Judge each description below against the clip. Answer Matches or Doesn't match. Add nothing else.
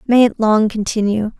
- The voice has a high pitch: Matches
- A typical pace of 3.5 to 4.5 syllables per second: Doesn't match